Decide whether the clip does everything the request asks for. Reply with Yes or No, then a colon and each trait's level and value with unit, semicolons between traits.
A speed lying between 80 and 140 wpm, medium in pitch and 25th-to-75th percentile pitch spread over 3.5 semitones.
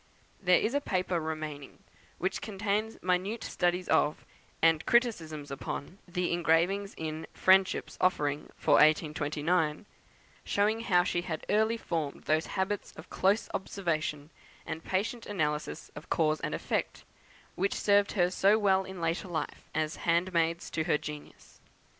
Yes: slow, 135 wpm; medium, 175 Hz; average, 4.0 semitones